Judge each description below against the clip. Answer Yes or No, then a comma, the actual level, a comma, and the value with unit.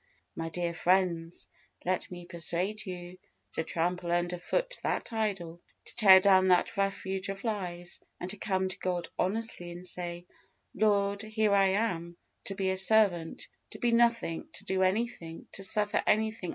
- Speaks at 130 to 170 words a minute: Yes, average, 165 wpm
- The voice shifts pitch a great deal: No, average, 3.0 semitones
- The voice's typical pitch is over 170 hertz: Yes, high, 190 Hz